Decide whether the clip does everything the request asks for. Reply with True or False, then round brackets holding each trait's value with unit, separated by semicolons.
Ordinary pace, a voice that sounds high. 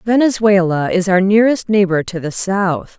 True (160 wpm; 195 Hz)